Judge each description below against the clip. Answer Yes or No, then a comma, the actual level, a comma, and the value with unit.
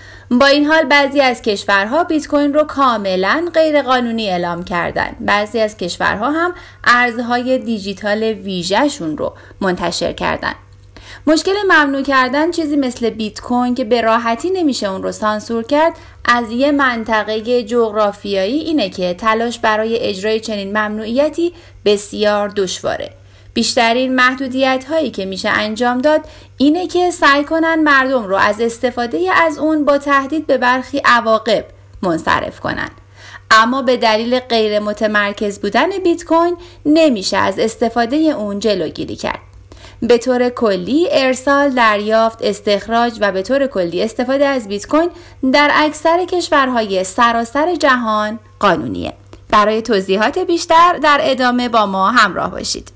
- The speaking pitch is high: Yes, high, 240 Hz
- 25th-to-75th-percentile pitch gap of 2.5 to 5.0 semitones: No, wide, 5.5 semitones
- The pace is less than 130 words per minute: No, average, 135 wpm